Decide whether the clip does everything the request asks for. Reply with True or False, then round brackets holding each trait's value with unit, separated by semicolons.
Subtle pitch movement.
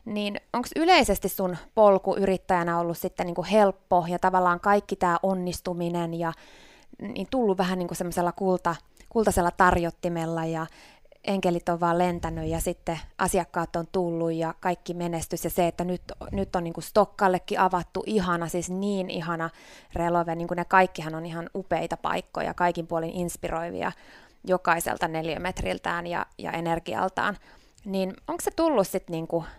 True (2.3 semitones)